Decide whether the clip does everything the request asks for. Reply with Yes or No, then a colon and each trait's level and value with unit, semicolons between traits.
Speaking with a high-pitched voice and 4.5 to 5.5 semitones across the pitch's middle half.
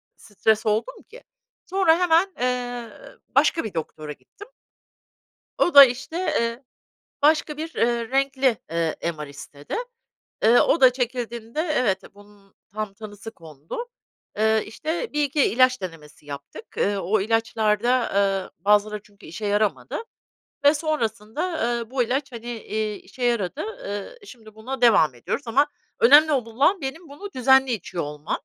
Yes: high, 230 Hz; average, 5.1 semitones